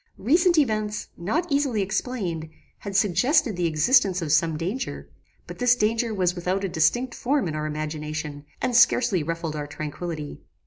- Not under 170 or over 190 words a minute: No, average, 155 wpm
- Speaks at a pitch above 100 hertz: Yes, high, 190 Hz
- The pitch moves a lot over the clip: Yes, wide, 7.4 semitones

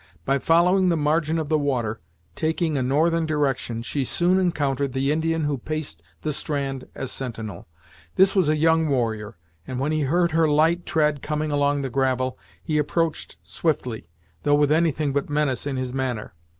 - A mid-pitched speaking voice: Yes, medium, 145 Hz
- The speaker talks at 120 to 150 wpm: No, average, 175 wpm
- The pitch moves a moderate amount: Yes, average, 3.3 semitones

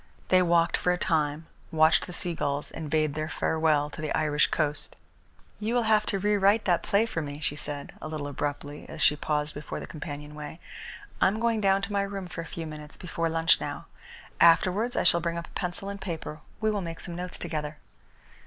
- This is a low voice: No, medium, 165 Hz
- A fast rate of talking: Yes, fast, 215 wpm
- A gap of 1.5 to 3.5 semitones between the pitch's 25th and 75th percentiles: No, average, 4.1 semitones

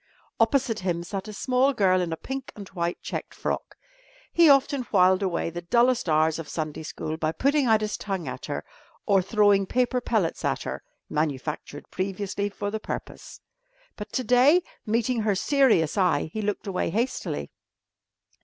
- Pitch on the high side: Yes, high, 205 Hz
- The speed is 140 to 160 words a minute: No, average, 170 wpm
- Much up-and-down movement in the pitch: Yes, wide, 6.0 semitones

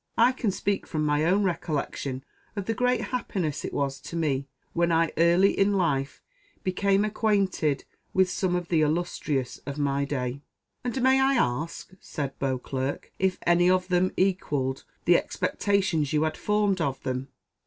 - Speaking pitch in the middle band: Yes, medium, 170 Hz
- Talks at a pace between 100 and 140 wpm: No, average, 165 wpm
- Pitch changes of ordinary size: No, wide, 5.7 semitones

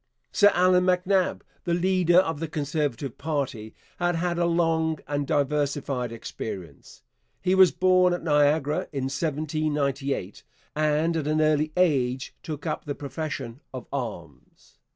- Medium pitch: Yes, medium, 150 Hz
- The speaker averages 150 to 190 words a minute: No, slow, 135 wpm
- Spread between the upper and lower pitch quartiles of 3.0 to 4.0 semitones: Yes, average, 3.7 semitones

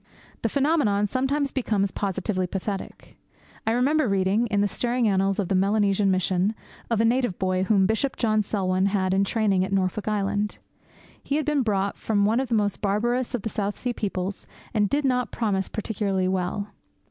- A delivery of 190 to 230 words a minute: No, average, 180 wpm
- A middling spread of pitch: Yes, average, 3.3 semitones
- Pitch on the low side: No, high, 205 Hz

